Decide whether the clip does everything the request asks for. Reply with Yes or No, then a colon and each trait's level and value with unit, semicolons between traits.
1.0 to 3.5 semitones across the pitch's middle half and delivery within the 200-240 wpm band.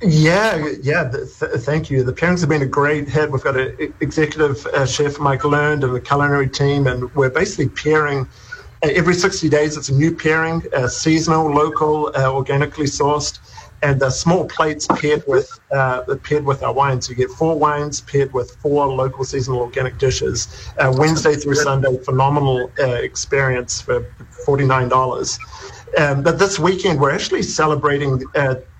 No: average, 2.7 semitones; average, 175 wpm